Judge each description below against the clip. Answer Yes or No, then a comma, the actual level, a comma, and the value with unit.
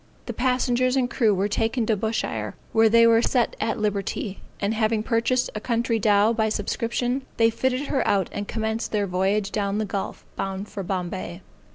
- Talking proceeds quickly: No, average, 185 wpm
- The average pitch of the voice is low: No, high, 220 Hz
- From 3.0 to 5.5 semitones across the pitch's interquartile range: No, narrow, 2.5 semitones